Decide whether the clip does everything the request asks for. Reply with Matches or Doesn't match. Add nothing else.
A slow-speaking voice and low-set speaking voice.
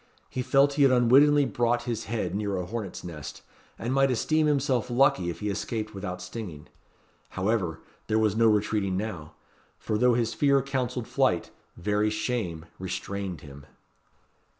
Doesn't match